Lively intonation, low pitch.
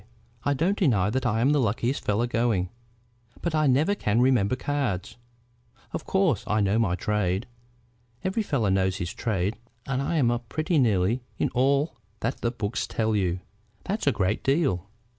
Yes: wide, 5.7 semitones; low, 120 Hz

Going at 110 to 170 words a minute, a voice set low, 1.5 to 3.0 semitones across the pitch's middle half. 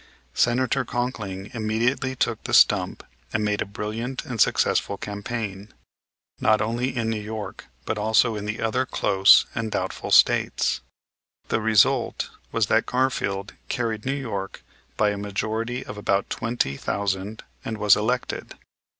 Yes: average, 140 wpm; low, 110 Hz; narrow, 2.6 semitones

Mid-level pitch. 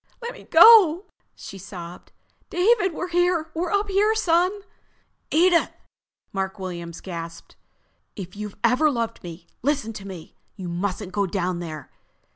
No: high, 225 Hz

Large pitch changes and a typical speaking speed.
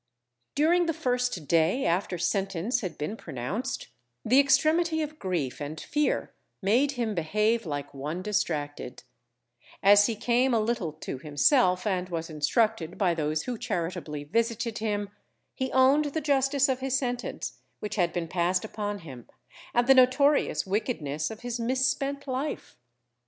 Yes: wide, 7.4 semitones; average, 150 wpm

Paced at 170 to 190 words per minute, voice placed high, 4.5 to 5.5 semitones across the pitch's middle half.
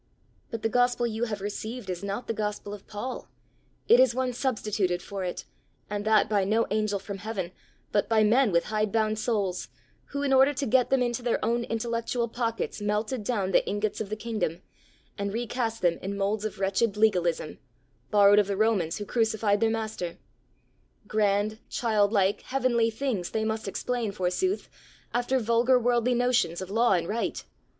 No: average, 180 wpm; high, 220 Hz; average, 2.8 semitones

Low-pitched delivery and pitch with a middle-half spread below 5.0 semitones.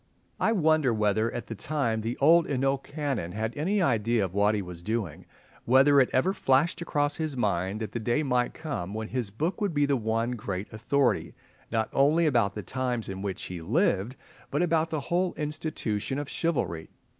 No: low, 125 Hz; wide, 5.6 semitones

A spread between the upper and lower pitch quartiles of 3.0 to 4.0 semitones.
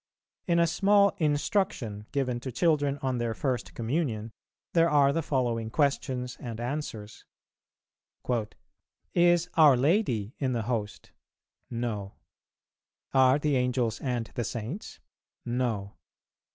No: average, 4.4 semitones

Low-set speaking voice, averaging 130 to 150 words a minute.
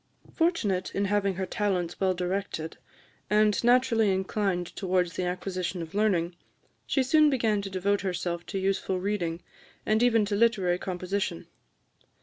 No: high, 195 Hz; average, 140 wpm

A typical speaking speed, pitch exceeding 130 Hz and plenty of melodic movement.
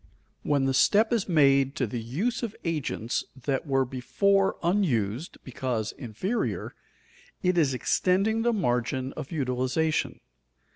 No: slow, 130 wpm; medium, 140 Hz; wide, 6.6 semitones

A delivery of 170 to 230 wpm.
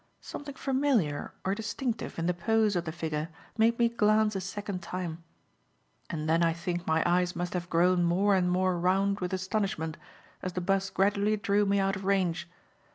Yes: average, 185 wpm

